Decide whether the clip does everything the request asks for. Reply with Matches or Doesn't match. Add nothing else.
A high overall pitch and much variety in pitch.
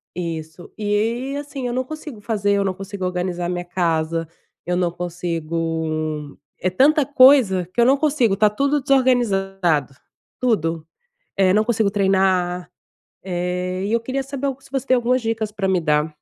Matches